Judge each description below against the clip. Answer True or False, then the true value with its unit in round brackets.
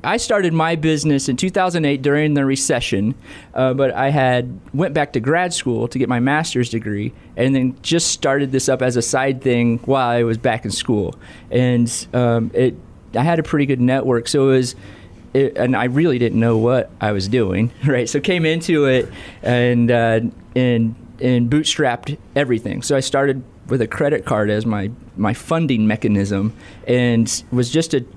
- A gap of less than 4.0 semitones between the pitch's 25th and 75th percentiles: True (3.3 semitones)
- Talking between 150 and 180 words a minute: False (190 wpm)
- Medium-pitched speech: False (125 Hz)